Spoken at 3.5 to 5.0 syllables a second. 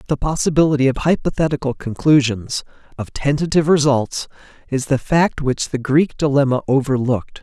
No: 5.4 syllables/s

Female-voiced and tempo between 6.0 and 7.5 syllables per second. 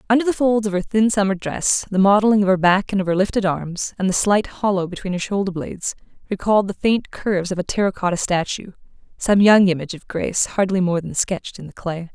Yes: female; 6.2 syllables/s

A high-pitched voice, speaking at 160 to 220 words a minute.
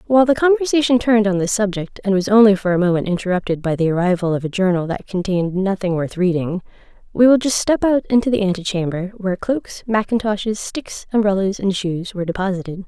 Yes: high, 200 Hz; average, 195 wpm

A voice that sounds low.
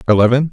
Yes: low, 125 Hz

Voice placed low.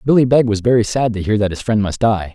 Yes: low, 110 Hz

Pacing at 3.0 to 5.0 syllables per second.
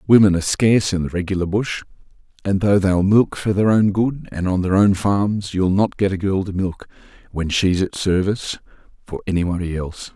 No: 5.4 syllables/s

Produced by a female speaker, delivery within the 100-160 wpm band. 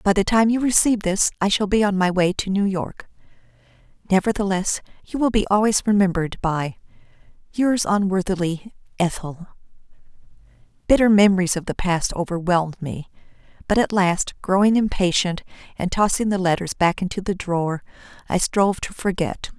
Yes: female; average, 150 wpm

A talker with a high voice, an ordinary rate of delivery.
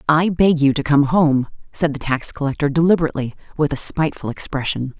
No: medium, 150 Hz; average, 180 wpm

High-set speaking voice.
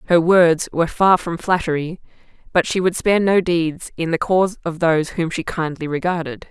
No: medium, 170 Hz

